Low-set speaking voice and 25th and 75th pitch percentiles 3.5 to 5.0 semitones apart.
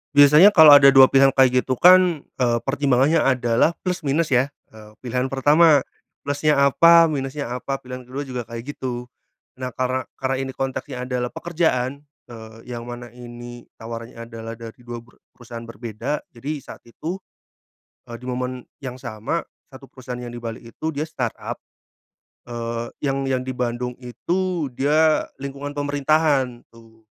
No: low, 130 Hz; average, 3.0 semitones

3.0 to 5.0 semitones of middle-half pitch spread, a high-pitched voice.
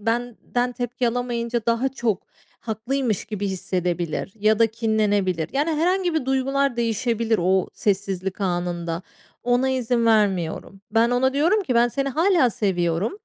Yes: average, 4.4 semitones; high, 230 Hz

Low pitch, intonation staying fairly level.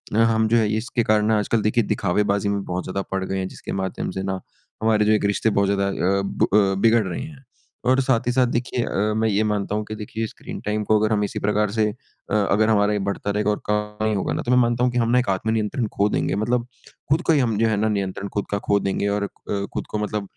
Yes: low, 105 Hz; narrow, 1.9 semitones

